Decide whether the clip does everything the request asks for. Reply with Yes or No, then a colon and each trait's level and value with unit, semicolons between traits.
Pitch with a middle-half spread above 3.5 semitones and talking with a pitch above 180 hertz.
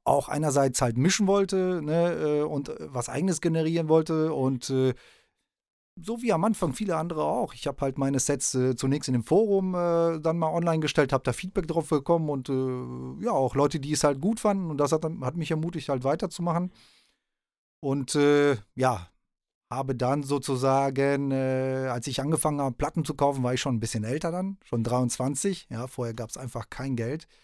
No: average, 4.1 semitones; medium, 145 Hz